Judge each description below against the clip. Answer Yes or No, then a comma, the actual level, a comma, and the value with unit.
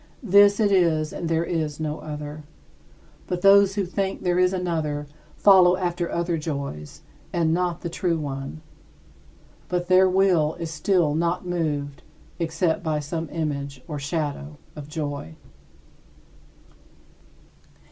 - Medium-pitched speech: Yes, medium, 165 Hz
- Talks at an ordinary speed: No, slow, 130 wpm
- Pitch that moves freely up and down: No, average, 3.1 semitones